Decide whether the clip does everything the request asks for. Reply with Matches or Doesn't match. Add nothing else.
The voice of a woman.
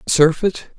Doesn't match